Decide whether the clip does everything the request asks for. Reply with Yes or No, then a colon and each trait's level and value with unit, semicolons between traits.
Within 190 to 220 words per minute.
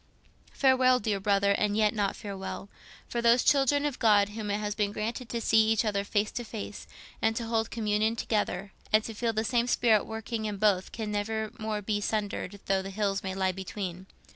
Yes: average, 200 wpm